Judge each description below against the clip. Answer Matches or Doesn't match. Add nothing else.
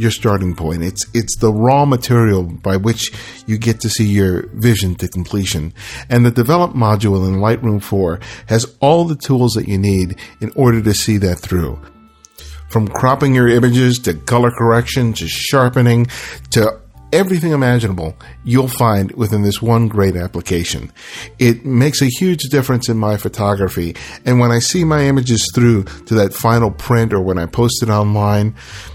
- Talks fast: Doesn't match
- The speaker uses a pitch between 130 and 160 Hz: Doesn't match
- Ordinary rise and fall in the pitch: Matches